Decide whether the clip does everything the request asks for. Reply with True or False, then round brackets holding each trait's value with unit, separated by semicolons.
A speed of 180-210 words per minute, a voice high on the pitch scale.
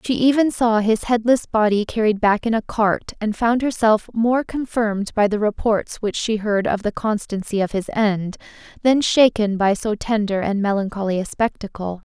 True (185 wpm; 215 Hz)